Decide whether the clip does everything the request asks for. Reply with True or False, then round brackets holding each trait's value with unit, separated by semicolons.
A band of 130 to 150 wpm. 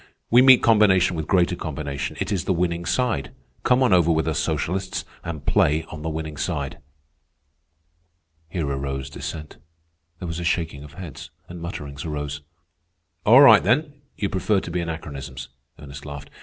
False (165 wpm)